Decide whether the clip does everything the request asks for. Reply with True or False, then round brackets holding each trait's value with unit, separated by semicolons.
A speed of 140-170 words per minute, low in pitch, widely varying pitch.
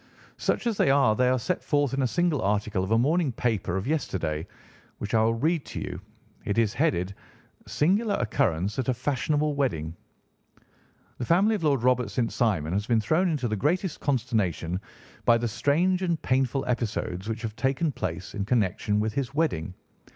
False (185 wpm; 120 Hz; 5.9 semitones)